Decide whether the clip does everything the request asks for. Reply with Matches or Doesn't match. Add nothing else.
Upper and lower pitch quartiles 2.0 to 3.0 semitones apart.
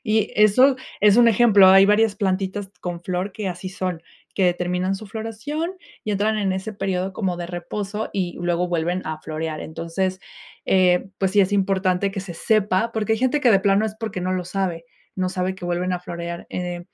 Matches